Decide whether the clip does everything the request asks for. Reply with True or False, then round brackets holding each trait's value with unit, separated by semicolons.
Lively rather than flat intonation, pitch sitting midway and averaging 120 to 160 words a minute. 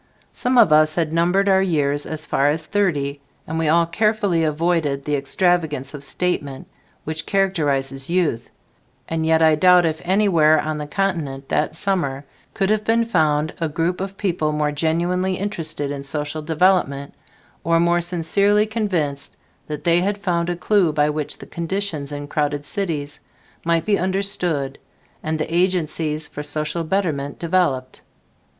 False (3.8 semitones; 160 Hz; 155 wpm)